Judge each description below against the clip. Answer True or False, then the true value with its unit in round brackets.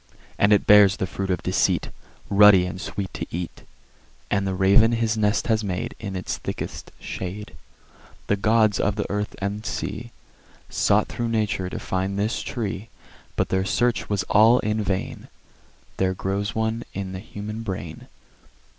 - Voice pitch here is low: True (100 Hz)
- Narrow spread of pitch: True (2.2 semitones)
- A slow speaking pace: False (165 wpm)